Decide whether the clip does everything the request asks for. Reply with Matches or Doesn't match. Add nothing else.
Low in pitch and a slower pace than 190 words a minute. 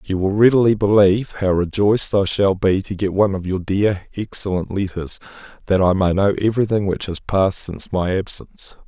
Doesn't match